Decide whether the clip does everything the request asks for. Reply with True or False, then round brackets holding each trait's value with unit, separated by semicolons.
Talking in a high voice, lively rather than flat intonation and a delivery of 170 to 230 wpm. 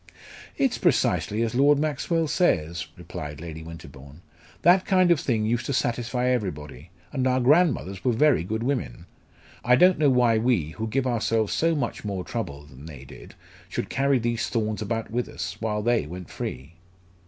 False (115 Hz; 6.7 semitones; 175 wpm)